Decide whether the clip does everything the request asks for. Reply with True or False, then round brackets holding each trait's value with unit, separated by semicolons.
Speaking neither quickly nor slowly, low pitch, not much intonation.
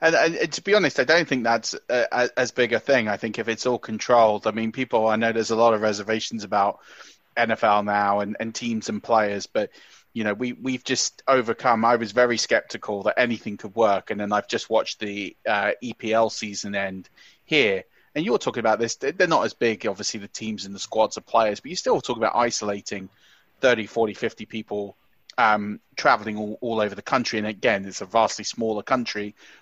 False (215 wpm; 110 Hz; 2.0 semitones)